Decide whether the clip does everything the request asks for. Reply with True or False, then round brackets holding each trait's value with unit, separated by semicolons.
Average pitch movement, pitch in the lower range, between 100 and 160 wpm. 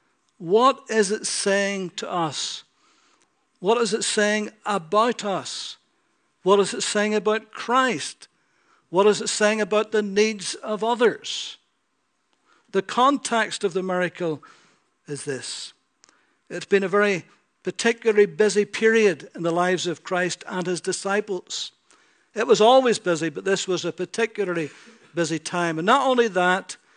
False (3.5 semitones; 205 Hz; 140 wpm)